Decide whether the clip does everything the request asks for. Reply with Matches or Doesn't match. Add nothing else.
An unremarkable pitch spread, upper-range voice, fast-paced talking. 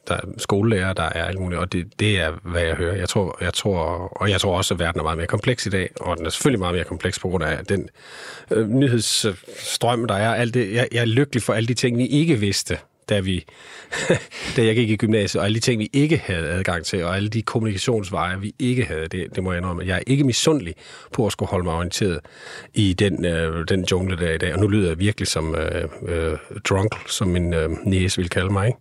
Doesn't match